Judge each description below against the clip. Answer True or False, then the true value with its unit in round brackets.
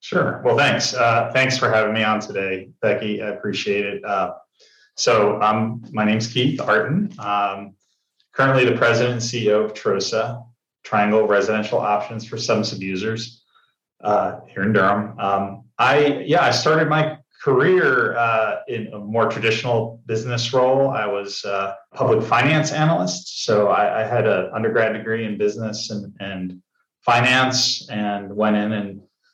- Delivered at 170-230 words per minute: False (155 wpm)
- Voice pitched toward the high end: False (110 Hz)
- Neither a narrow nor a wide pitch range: True (3.4 semitones)